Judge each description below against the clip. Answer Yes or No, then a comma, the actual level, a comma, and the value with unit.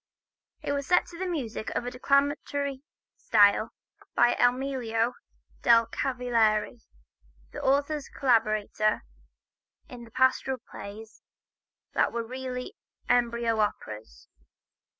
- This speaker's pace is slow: Yes, slow, 100 wpm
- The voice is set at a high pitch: Yes, high, 245 Hz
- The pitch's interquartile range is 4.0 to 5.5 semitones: No, average, 3.2 semitones